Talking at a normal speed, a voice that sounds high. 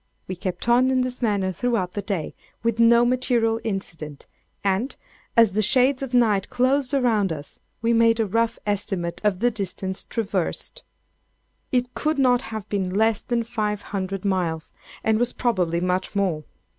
Yes: average, 165 wpm; high, 215 Hz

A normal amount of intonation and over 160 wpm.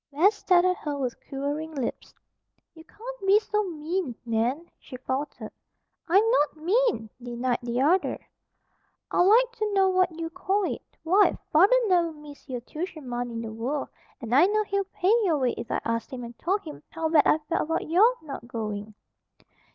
No: wide, 7.0 semitones; average, 185 wpm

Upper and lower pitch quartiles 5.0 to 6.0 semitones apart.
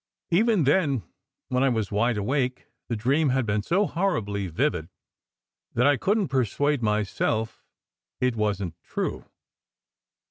Yes: wide, 5.5 semitones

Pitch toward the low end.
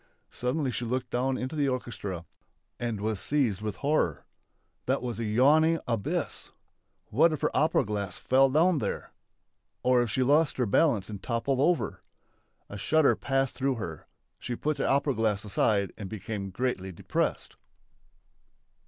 Yes: low, 125 Hz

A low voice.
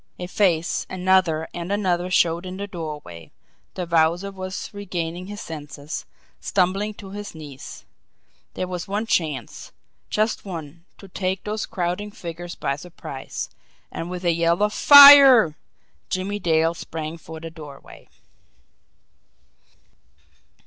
No: medium, 175 Hz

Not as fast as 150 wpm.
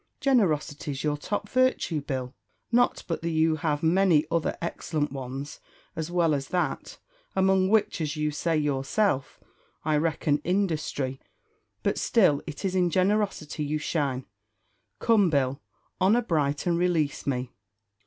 Yes: average, 140 wpm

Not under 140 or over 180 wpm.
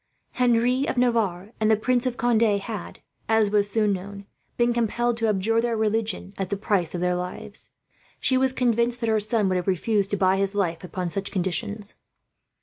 No: average, 195 wpm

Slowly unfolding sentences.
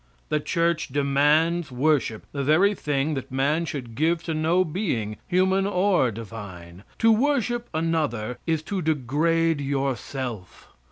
Yes: slow, 130 wpm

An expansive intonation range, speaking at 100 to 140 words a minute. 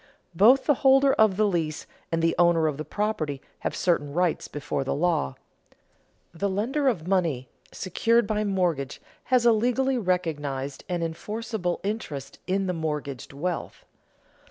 No: wide, 5.8 semitones; average, 150 wpm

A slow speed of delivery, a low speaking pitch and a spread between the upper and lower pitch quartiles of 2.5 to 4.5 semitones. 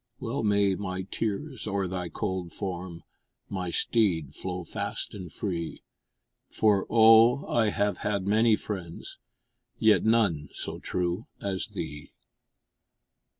Yes: slow, 120 wpm; low, 100 Hz; average, 3.4 semitones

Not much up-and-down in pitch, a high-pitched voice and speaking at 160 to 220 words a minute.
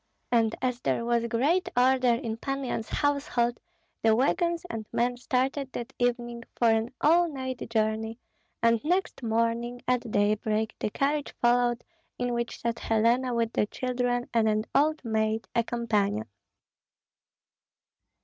No: narrow, 2.3 semitones; high, 240 Hz; average, 140 wpm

